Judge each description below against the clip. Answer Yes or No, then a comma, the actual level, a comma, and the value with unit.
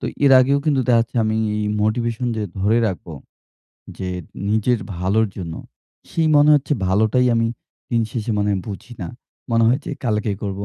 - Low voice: Yes, low, 110 Hz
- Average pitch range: Yes, average, 3.2 semitones